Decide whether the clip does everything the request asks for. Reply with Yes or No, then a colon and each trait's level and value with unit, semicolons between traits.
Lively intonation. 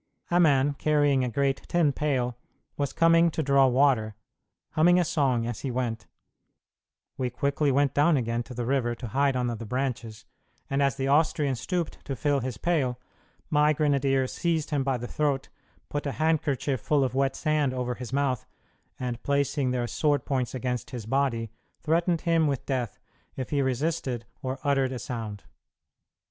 No: average, 2.9 semitones